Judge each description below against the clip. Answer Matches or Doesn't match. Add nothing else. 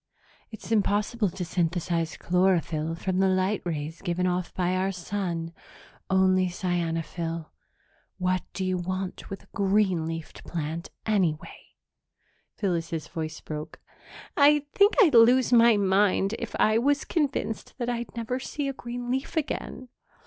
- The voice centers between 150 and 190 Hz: Matches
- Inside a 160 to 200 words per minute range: Doesn't match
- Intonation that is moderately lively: Matches